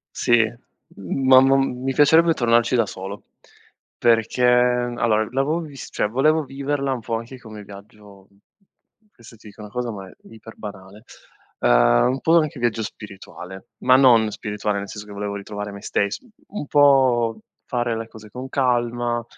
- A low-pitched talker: Yes, low, 115 Hz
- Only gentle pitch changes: No, average, 4.0 semitones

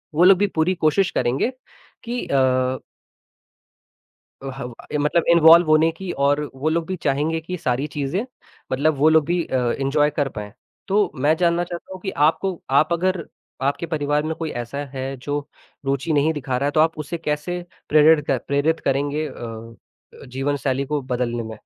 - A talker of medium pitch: Yes, medium, 150 Hz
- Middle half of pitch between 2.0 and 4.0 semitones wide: Yes, average, 3.5 semitones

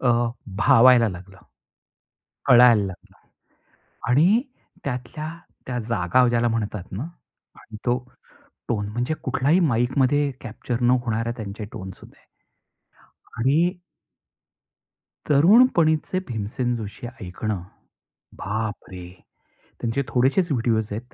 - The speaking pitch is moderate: No, low, 120 Hz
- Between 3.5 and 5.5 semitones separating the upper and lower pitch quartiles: Yes, average, 3.8 semitones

